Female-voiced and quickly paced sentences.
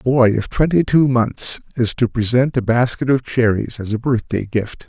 No: male; fast, 210 wpm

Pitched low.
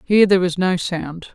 No: medium, 180 Hz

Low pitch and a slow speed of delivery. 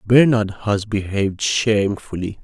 Yes: low, 105 Hz; slow, 100 wpm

